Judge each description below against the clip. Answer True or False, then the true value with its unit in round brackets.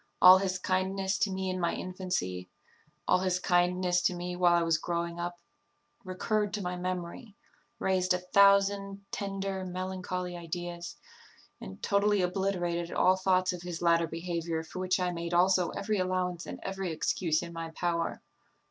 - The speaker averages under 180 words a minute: True (160 wpm)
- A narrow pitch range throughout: True (1.6 semitones)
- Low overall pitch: False (180 Hz)